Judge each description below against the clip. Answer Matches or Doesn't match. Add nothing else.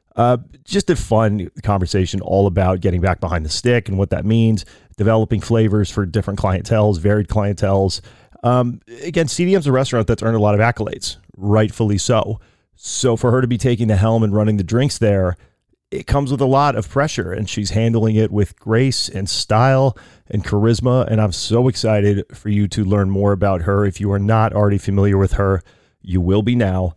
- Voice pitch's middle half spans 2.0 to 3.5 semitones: Matches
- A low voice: Matches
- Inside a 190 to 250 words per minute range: Matches